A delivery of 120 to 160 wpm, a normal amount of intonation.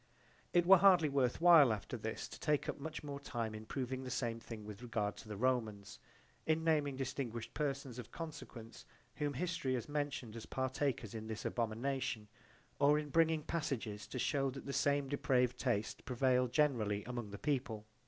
No: average, 175 wpm; average, 4.2 semitones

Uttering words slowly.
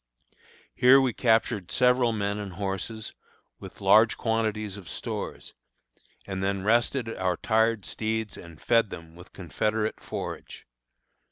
Yes: slow, 125 wpm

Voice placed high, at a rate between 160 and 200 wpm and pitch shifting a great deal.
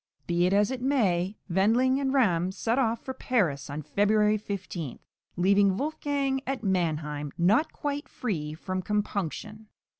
No: high, 205 Hz; average, 145 wpm; wide, 6.3 semitones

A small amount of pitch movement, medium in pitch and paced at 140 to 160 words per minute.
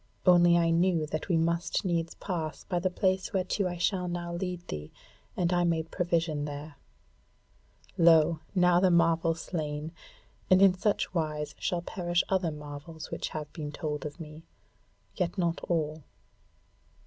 Yes: narrow, 2.3 semitones; medium, 170 Hz; average, 155 wpm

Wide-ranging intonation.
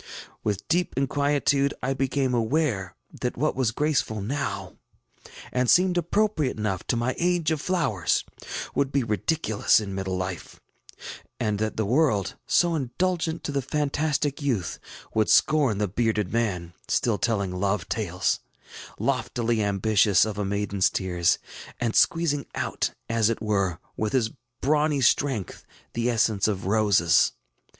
Yes: wide, 5.9 semitones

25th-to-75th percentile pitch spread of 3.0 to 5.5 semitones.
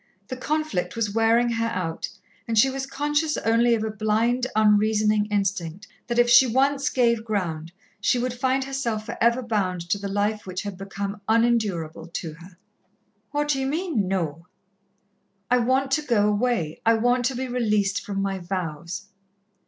Yes: average, 4.2 semitones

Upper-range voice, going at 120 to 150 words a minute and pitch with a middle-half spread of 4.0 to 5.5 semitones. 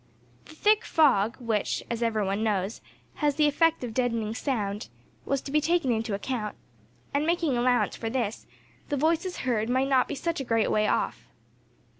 No: high, 245 Hz; average, 180 wpm; average, 5.0 semitones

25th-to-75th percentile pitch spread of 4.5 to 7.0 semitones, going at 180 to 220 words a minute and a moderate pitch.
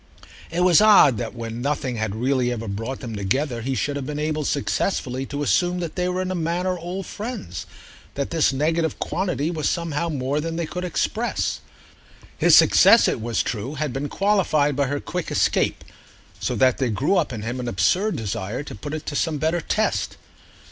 Yes: wide, 5.5 semitones; average, 190 wpm; medium, 145 Hz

